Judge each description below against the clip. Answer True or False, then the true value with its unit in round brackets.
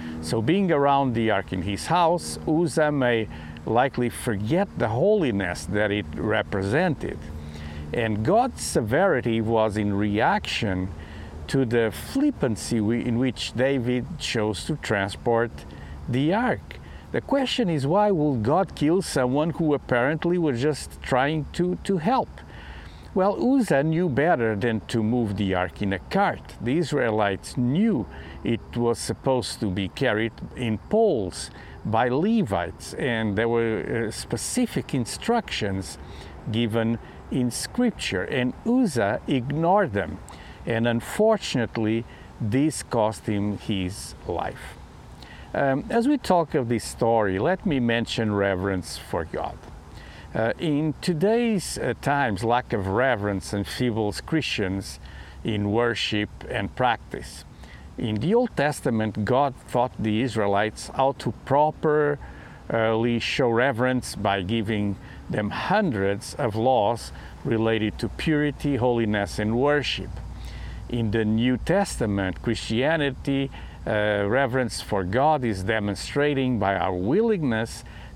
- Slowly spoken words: True (125 wpm)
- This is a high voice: False (115 Hz)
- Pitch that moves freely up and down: True (6.1 semitones)